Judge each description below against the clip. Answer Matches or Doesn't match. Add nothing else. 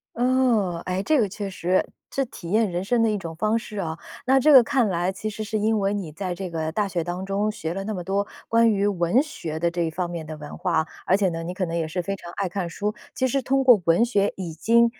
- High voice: Matches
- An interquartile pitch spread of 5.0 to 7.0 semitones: Doesn't match